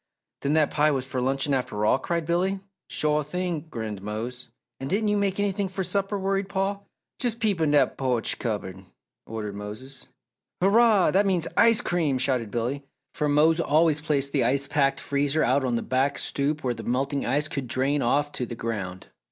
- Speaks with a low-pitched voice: No, medium, 145 Hz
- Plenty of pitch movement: Yes, wide, 5.8 semitones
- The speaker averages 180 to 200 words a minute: Yes, average, 190 wpm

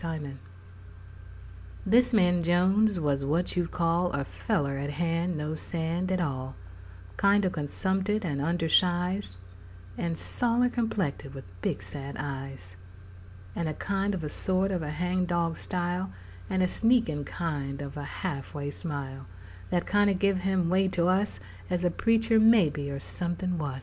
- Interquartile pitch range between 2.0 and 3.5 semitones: No, average, 4.6 semitones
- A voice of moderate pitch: Yes, medium, 175 Hz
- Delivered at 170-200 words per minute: No, average, 160 wpm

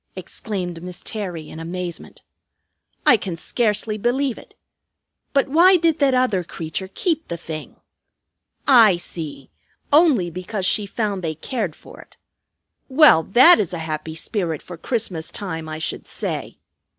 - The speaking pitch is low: No, high, 190 Hz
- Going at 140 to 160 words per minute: Yes, average, 145 wpm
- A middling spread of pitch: No, wide, 6.8 semitones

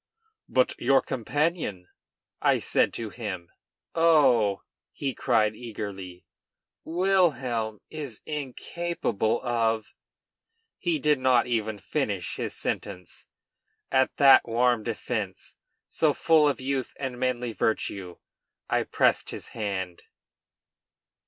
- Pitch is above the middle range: No, low, 120 Hz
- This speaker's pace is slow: Yes, slow, 105 wpm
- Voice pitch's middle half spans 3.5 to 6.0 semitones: Yes, average, 5.2 semitones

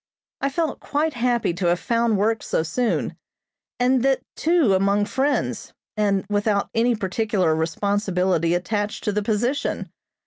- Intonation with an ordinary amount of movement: Yes, average, 4.2 semitones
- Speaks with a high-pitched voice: Yes, high, 210 Hz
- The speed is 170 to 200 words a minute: No, average, 140 wpm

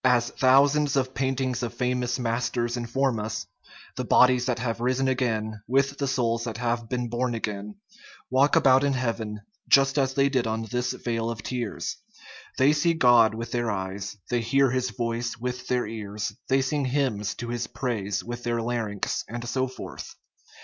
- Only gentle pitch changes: Yes, narrow, 2.2 semitones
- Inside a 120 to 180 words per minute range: Yes, average, 175 wpm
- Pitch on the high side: No, low, 120 Hz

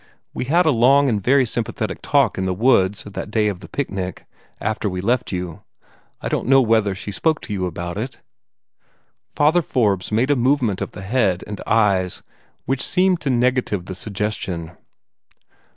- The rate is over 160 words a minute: Yes, average, 175 wpm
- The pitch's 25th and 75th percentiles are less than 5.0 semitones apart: No, wide, 5.4 semitones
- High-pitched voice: No, low, 110 Hz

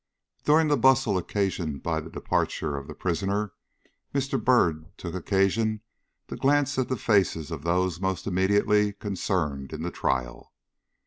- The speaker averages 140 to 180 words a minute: Yes, average, 145 wpm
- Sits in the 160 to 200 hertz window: No, very low, 95 Hz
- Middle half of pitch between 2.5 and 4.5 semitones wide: No, average, 5.0 semitones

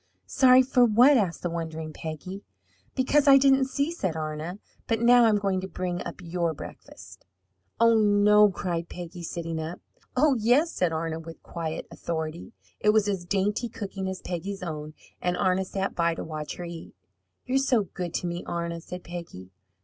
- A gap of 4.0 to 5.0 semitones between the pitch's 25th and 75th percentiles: Yes, average, 4.7 semitones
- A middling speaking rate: Yes, average, 180 wpm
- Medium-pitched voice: Yes, medium, 180 Hz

